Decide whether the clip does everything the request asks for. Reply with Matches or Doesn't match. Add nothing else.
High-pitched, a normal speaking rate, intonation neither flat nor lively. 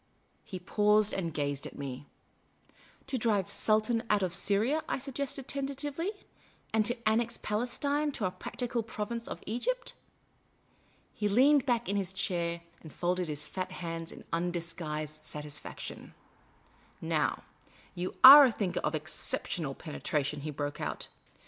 Doesn't match